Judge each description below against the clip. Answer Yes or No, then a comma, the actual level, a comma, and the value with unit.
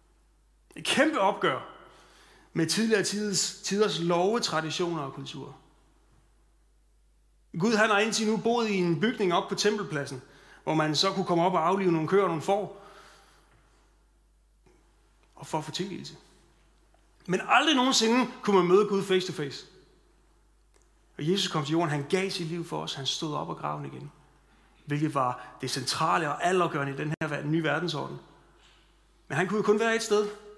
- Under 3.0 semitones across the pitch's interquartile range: No, average, 5.0 semitones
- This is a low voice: No, medium, 175 Hz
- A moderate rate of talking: Yes, average, 175 wpm